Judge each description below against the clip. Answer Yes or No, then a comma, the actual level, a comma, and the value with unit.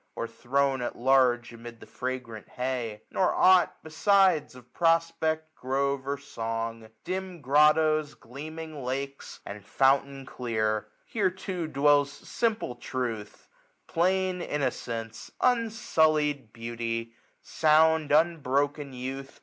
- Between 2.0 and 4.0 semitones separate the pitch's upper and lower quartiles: No, average, 4.6 semitones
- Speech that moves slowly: Yes, slow, 110 wpm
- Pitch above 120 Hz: Yes, medium, 140 Hz